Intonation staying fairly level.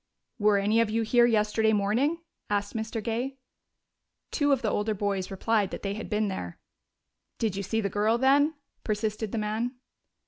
Yes: narrow, 2.1 semitones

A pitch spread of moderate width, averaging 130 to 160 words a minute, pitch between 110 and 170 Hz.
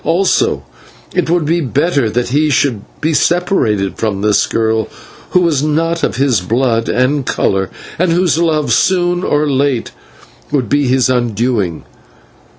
No: wide, 6.2 semitones; average, 150 wpm; medium, 140 Hz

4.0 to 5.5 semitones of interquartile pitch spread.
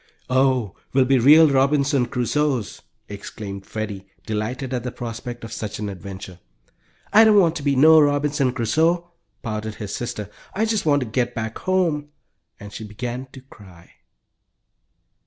Yes: average, 5.2 semitones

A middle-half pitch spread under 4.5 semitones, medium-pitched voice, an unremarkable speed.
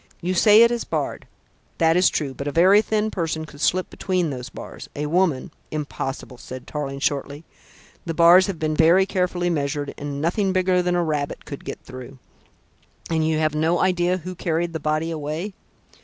Yes: average, 3.7 semitones; medium, 165 Hz; average, 190 wpm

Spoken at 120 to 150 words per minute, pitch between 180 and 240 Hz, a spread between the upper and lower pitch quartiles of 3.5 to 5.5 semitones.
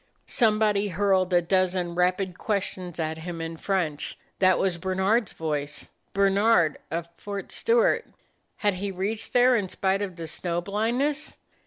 No: average, 145 wpm; high, 190 Hz; average, 2.9 semitones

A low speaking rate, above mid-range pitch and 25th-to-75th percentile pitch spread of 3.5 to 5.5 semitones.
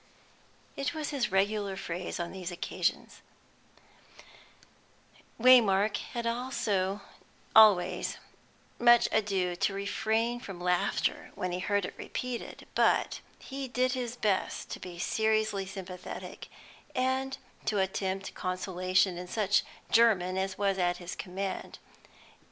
Yes: slow, 115 wpm; high, 195 Hz; average, 4.0 semitones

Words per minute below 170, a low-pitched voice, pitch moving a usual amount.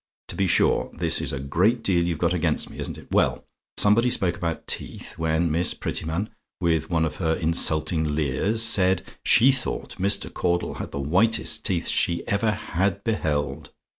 No: average, 175 wpm; very low, 85 Hz; average, 4.0 semitones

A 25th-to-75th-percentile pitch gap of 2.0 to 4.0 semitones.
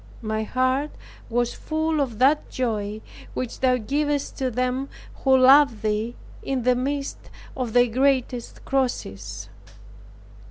Yes: narrow, 2.5 semitones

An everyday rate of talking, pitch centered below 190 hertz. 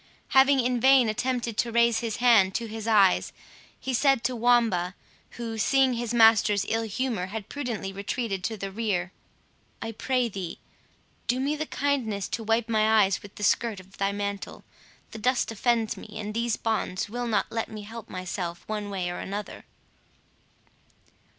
No: average, 170 wpm; high, 225 Hz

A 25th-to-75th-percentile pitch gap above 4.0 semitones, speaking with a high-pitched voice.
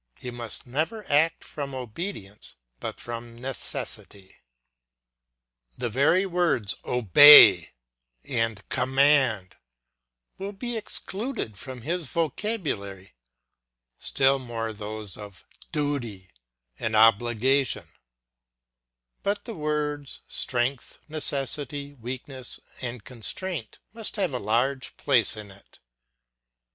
No: average, 5.0 semitones; low, 130 Hz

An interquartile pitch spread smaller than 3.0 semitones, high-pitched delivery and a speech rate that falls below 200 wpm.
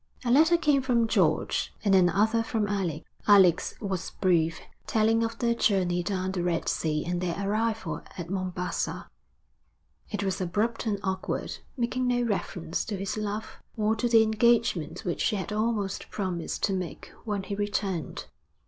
No: average, 3.8 semitones; high, 200 Hz; average, 160 wpm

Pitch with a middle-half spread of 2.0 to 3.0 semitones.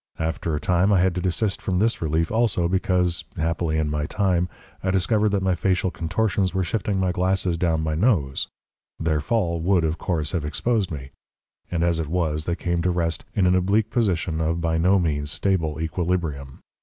Yes: average, 2.7 semitones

